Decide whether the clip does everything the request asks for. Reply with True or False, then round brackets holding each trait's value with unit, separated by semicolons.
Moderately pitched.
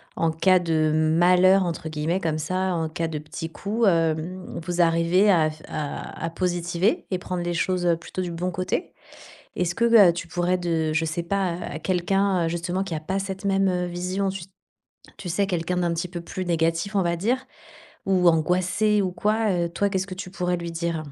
True (175 Hz)